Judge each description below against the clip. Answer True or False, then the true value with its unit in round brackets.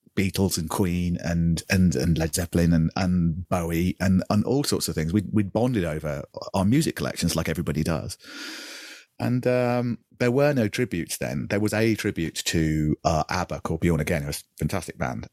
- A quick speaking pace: False (190 wpm)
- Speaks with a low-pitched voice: True (90 Hz)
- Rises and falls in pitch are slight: False (4.4 semitones)